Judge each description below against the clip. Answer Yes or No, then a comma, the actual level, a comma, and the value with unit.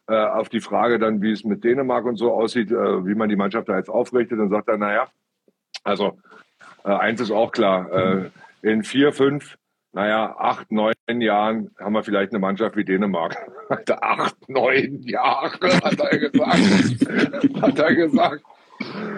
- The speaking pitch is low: Yes, low, 110 Hz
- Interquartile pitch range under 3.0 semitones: Yes, narrow, 2.4 semitones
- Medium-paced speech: Yes, average, 155 wpm